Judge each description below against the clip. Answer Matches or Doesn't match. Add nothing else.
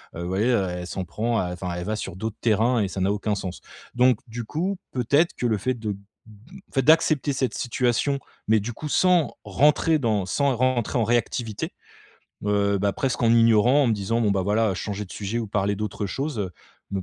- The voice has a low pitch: Matches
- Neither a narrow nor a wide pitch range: Matches